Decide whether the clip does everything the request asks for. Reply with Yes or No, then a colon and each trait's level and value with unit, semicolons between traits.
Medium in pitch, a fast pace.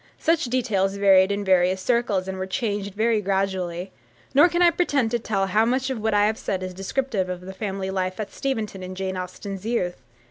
No: high, 200 Hz; fast, 210 wpm